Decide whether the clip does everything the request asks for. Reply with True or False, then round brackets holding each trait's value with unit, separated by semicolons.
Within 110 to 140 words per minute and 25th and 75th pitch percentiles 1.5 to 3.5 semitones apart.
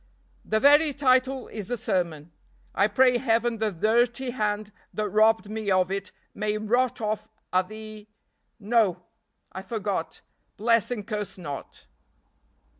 True (135 wpm; 2.9 semitones)